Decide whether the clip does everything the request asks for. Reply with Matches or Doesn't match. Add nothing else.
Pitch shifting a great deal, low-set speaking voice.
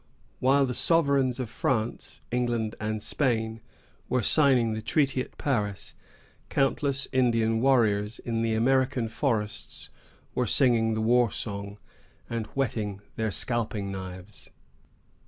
Doesn't match